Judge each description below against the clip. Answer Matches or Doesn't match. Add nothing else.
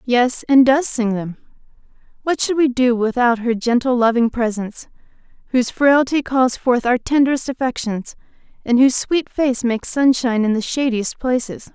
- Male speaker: Doesn't match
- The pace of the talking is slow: Doesn't match